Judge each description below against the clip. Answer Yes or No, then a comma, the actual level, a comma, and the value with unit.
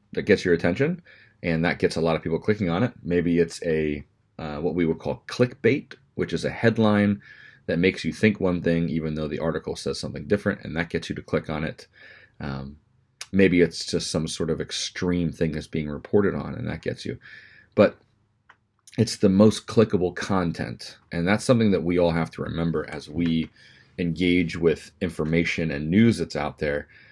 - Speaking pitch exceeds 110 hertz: No, very low, 85 Hz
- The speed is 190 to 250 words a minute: Yes, average, 200 wpm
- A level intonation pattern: No, average, 3.8 semitones